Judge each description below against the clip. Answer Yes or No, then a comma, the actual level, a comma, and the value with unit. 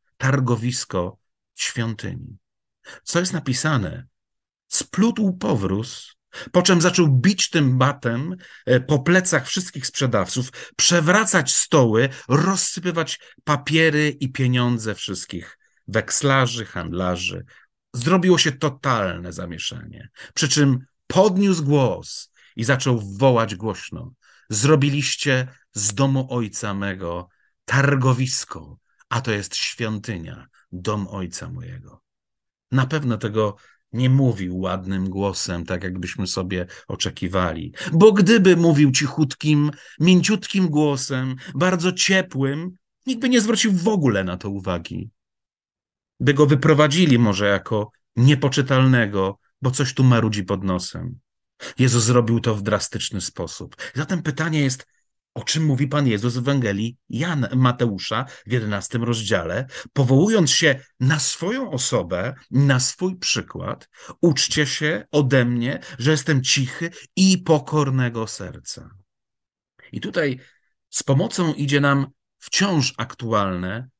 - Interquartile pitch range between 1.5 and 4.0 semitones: No, wide, 5.4 semitones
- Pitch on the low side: Yes, low, 130 Hz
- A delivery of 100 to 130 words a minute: Yes, average, 115 wpm